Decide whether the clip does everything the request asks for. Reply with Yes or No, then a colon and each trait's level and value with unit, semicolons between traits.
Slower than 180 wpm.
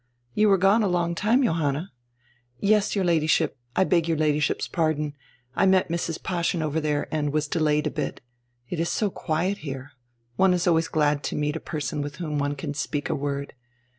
No: fast, 205 wpm